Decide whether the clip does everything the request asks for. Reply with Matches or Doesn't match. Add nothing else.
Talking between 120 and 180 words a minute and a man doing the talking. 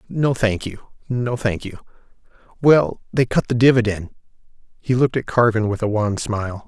Matches